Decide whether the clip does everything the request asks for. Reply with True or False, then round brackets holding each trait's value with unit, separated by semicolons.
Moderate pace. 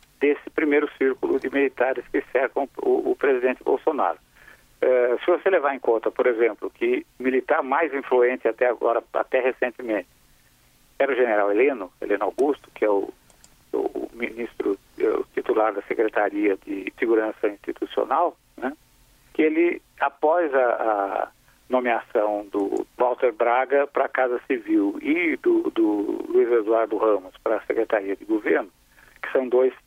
True (145 wpm)